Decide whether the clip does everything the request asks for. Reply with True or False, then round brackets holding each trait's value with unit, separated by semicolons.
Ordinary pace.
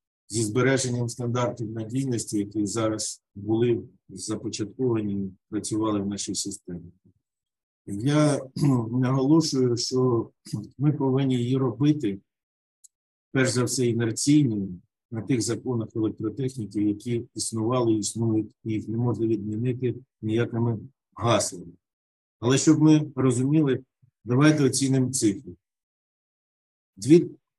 False (100 wpm)